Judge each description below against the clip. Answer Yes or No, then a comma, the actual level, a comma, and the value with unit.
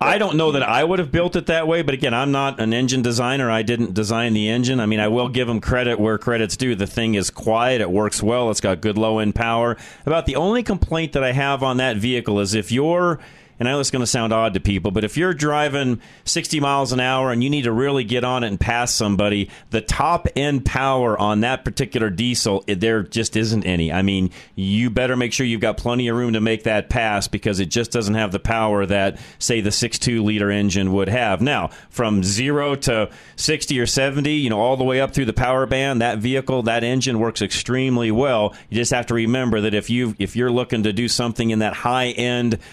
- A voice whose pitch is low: Yes, low, 120 Hz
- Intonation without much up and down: No, average, 3.3 semitones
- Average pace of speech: No, fast, 240 wpm